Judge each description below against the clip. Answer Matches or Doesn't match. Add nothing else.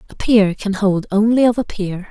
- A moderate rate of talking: Doesn't match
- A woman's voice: Matches